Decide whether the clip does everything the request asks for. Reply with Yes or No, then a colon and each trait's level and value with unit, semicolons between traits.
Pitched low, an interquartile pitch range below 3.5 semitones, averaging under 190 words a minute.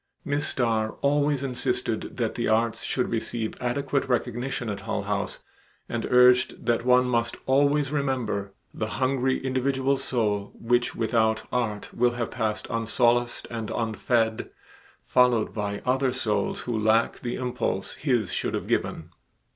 Yes: low, 120 Hz; average, 2.8 semitones; average, 140 wpm